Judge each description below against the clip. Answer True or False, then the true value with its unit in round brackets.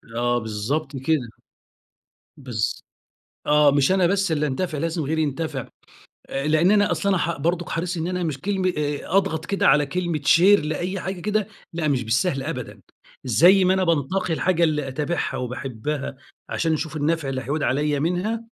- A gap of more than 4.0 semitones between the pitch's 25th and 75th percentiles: True (4.4 semitones)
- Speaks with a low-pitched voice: False (155 Hz)